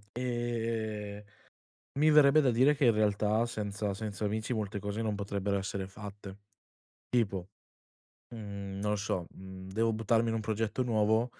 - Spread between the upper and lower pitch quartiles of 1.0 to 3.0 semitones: Yes, narrow, 2.4 semitones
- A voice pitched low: Yes, low, 105 Hz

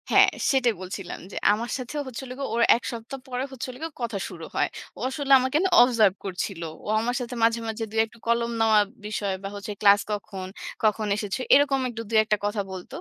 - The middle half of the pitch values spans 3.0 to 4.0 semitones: Yes, average, 3.5 semitones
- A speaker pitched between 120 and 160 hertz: No, high, 225 Hz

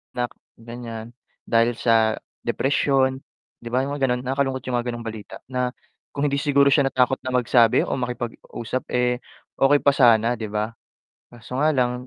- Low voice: Yes, low, 125 Hz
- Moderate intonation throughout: No, narrow, 2.2 semitones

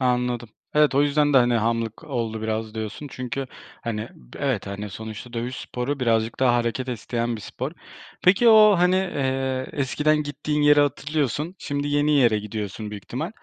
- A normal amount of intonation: Yes, average, 4.5 semitones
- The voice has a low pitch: Yes, low, 125 Hz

